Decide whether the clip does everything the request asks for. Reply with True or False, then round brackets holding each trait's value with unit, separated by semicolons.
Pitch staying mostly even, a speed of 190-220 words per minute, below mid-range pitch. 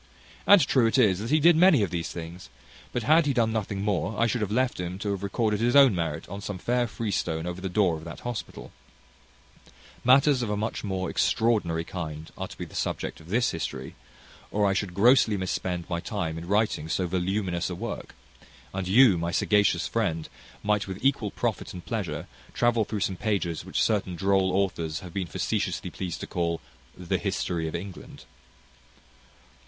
False (4.4 semitones; 195 wpm; 100 Hz)